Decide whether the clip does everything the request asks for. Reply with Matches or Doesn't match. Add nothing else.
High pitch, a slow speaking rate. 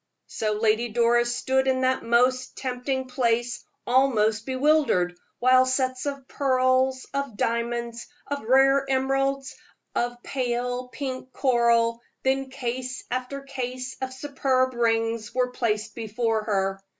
Matches